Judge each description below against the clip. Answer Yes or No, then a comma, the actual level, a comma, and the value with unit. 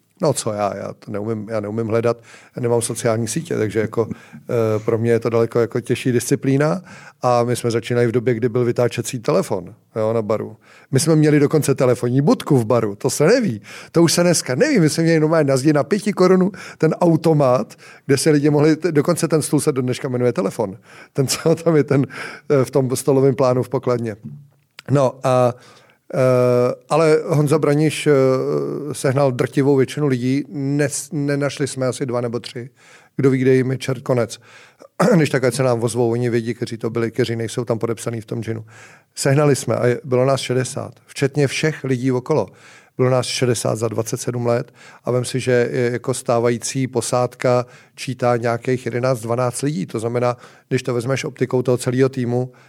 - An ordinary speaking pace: No, fast, 190 wpm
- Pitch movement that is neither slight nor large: Yes, average, 3.0 semitones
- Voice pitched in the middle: No, low, 130 Hz